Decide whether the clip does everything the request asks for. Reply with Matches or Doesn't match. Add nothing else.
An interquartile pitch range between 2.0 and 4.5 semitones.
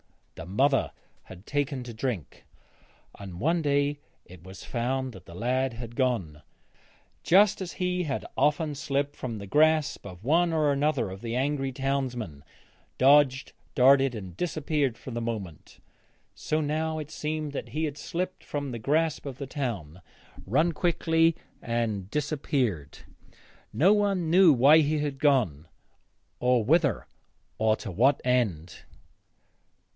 Doesn't match